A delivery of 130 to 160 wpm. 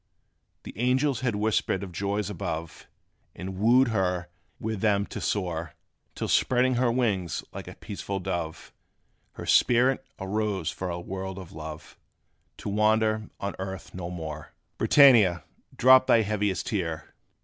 Yes: average, 140 wpm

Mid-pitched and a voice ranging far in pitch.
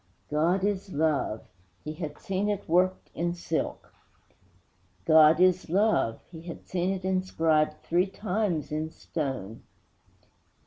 No: medium, 170 Hz; average, 3.3 semitones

